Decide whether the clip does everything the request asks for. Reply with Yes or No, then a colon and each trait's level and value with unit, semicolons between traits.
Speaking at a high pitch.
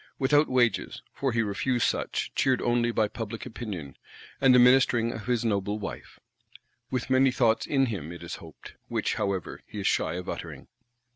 No: low, 115 Hz